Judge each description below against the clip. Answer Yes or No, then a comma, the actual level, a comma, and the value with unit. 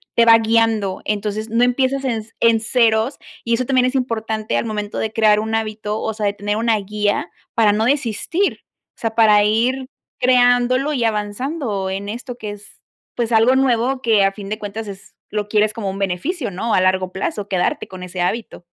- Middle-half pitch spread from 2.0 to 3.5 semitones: Yes, average, 2.7 semitones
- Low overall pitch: No, high, 220 Hz